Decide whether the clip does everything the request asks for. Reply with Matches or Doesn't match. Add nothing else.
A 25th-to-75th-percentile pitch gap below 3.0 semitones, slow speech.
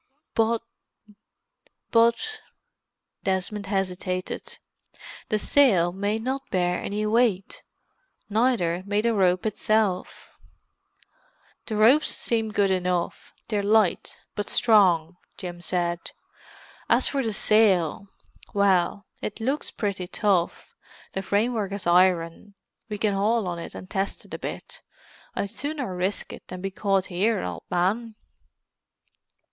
Doesn't match